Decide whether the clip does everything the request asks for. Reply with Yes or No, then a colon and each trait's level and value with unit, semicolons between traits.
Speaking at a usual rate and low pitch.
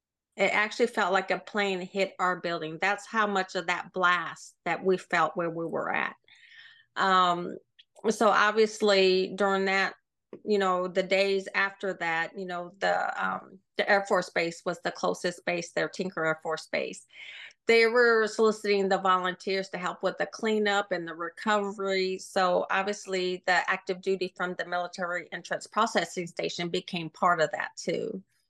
No: average, 165 wpm; high, 190 Hz